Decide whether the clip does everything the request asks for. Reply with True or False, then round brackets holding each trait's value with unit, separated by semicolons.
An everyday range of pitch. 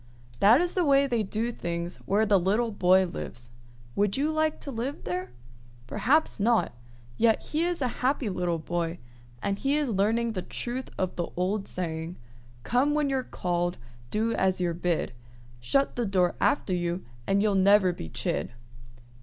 False (5.9 semitones)